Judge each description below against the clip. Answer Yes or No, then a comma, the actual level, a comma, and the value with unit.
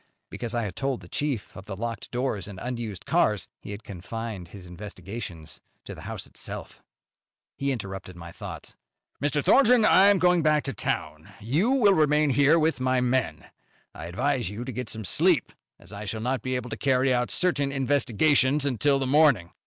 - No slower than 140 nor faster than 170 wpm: No, average, 190 wpm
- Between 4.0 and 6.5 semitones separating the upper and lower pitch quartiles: Yes, wide, 5.6 semitones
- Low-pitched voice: Yes, low, 125 Hz